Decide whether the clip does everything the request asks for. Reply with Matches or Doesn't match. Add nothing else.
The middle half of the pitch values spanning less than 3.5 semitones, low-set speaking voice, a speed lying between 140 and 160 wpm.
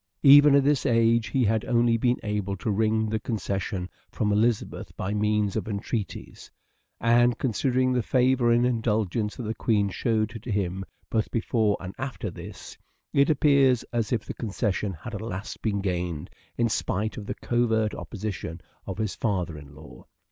Doesn't match